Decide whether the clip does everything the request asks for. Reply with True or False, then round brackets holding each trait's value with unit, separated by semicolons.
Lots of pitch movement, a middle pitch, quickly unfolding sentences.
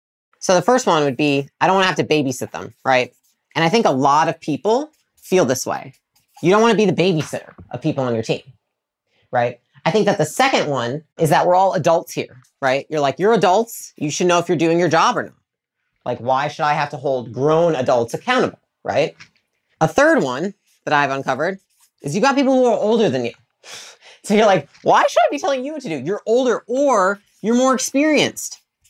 True (7.1 semitones; 165 Hz; 225 wpm)